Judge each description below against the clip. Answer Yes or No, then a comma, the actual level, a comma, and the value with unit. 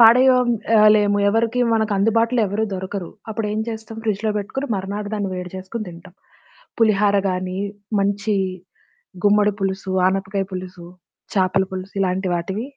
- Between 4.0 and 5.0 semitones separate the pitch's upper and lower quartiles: No, average, 2.7 semitones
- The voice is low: No, high, 205 Hz